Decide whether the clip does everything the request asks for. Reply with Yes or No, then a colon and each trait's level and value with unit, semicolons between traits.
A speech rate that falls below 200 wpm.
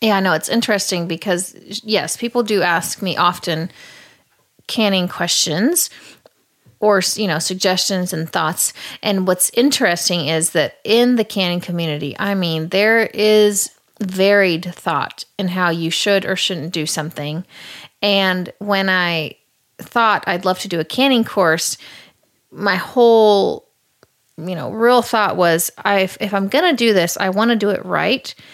Yes: average, 155 wpm